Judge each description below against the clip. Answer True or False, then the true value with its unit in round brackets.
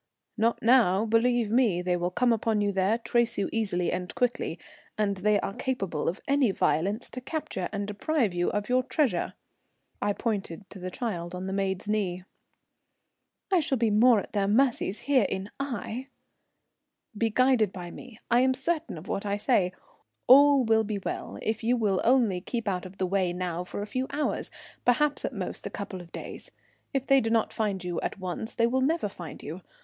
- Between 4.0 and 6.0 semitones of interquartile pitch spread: True (4.6 semitones)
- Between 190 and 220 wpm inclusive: True (195 wpm)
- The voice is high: True (215 Hz)